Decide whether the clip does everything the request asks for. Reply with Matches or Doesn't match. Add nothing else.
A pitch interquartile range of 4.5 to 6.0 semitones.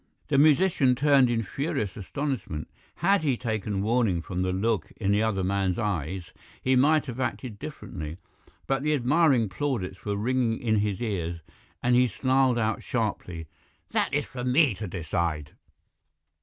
Matches